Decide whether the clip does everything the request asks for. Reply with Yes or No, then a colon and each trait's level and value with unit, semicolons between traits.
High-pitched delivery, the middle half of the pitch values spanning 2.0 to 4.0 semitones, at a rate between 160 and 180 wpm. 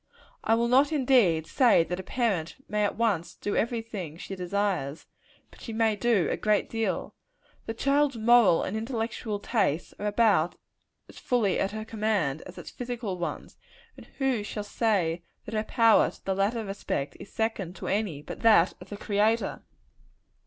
Yes: high, 210 Hz; average, 3.6 semitones; average, 175 wpm